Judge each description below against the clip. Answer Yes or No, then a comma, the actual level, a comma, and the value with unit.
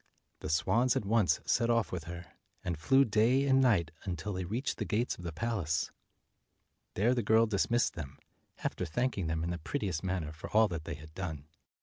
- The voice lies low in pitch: Yes, very low, 95 Hz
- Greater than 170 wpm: Yes, average, 200 wpm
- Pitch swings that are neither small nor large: No, wide, 6.0 semitones